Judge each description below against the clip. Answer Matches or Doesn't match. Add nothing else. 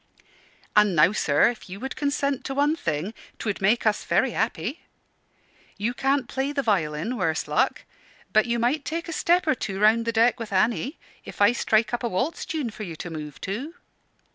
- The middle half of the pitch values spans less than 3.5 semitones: Doesn't match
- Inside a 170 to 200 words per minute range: Matches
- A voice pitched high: Matches